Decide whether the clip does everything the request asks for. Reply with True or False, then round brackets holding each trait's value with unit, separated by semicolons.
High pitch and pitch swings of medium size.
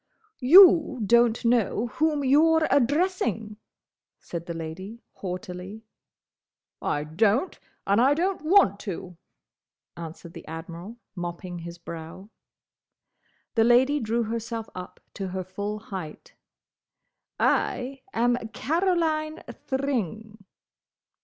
False (225 Hz; 7.3 semitones)